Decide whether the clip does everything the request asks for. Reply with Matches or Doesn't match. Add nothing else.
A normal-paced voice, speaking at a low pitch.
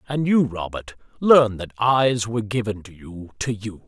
Matches